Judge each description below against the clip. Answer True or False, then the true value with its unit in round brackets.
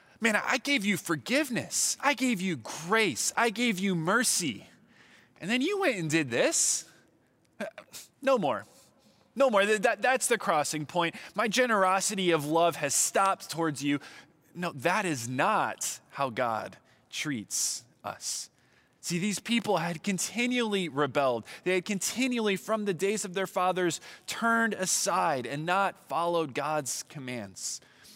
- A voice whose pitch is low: False (190 Hz)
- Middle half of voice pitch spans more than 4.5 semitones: True (5.6 semitones)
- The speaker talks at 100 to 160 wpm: True (145 wpm)